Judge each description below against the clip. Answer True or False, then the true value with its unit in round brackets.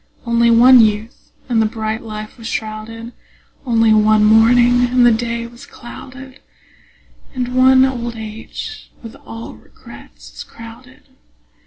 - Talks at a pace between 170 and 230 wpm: False (135 wpm)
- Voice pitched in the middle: False (230 Hz)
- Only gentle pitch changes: True (1.8 semitones)